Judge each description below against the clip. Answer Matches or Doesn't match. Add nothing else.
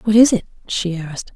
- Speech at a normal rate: Doesn't match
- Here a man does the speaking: Doesn't match